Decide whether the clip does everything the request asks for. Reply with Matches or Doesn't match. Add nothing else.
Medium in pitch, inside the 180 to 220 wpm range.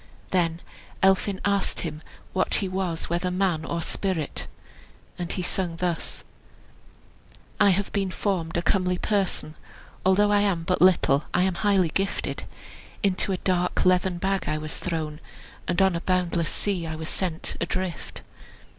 Doesn't match